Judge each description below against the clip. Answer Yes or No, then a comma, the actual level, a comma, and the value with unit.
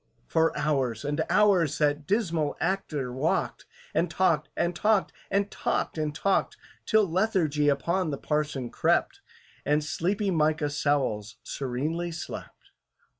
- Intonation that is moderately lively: Yes, average, 3.8 semitones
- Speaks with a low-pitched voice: No, medium, 155 Hz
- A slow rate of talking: Yes, slow, 125 wpm